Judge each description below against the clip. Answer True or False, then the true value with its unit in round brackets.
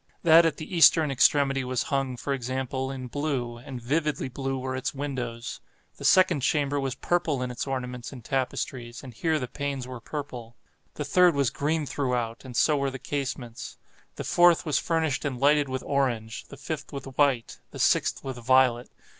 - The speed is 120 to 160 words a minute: False (175 wpm)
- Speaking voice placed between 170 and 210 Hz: False (135 Hz)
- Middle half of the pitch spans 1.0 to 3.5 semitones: True (2.5 semitones)